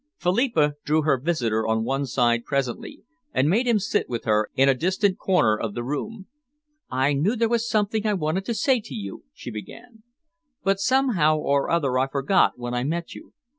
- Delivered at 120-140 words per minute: No, average, 195 wpm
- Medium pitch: Yes, medium, 155 Hz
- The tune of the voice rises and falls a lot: Yes, wide, 8.3 semitones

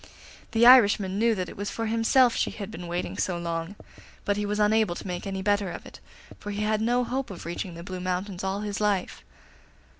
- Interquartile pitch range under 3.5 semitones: Yes, average, 3.0 semitones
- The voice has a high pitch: Yes, high, 205 Hz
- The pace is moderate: No, fast, 220 wpm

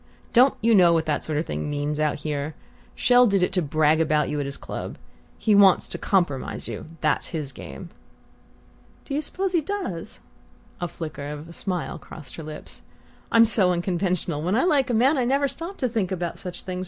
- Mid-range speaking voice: Yes, medium, 180 Hz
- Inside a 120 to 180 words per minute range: No, fast, 205 wpm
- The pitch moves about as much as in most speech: No, wide, 7.3 semitones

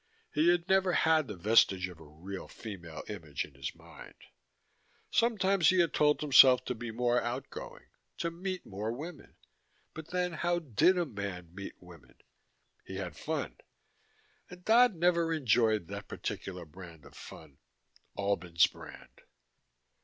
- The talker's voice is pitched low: Yes, low, 120 Hz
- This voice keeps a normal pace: Yes, average, 155 wpm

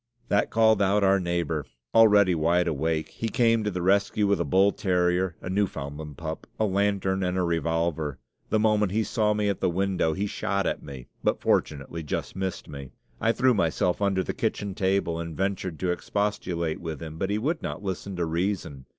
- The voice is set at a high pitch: No, very low, 95 Hz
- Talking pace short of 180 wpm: No, average, 195 wpm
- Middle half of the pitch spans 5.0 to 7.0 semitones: No, average, 3.6 semitones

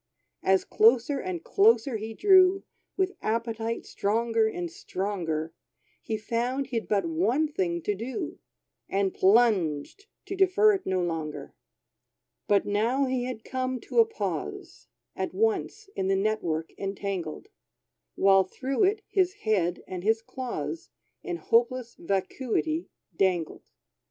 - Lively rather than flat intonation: Yes, wide, 6.4 semitones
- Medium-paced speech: No, slow, 130 wpm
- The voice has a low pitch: No, high, 225 Hz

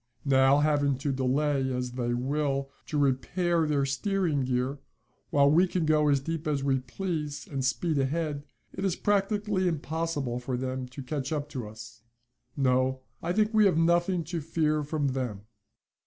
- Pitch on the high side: No, medium, 145 Hz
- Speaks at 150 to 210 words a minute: Yes, average, 170 wpm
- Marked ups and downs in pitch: No, average, 3.9 semitones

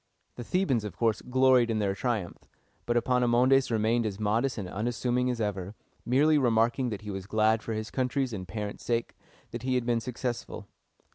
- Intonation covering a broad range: No, average, 2.7 semitones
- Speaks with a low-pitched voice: Yes, low, 115 Hz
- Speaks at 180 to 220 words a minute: Yes, average, 185 wpm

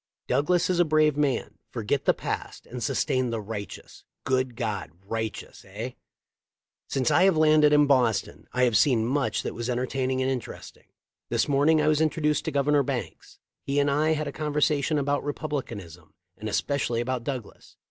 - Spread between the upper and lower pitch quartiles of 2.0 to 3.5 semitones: No, average, 3.9 semitones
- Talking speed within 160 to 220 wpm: Yes, average, 180 wpm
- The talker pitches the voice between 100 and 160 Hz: Yes, low, 135 Hz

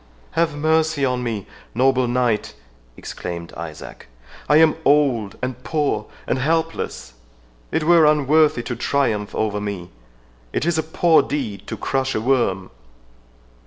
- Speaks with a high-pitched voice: No, low, 130 Hz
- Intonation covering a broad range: Yes, wide, 6.6 semitones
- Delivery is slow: Yes, slow, 130 wpm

